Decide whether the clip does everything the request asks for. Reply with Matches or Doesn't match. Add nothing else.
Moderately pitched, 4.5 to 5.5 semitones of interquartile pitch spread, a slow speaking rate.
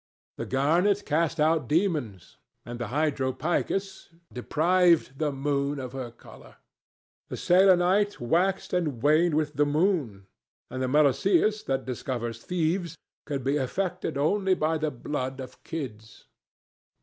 Matches